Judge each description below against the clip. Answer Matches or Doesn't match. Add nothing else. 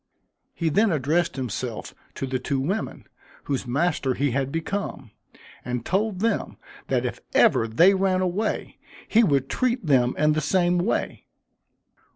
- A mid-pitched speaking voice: Matches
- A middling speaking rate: Matches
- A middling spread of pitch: Doesn't match